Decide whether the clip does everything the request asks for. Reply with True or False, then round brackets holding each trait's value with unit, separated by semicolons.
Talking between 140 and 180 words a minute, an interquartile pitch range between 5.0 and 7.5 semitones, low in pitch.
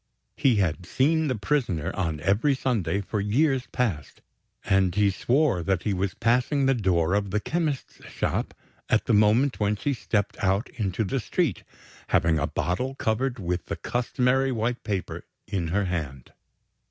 True (165 wpm; 5.6 semitones; 105 Hz)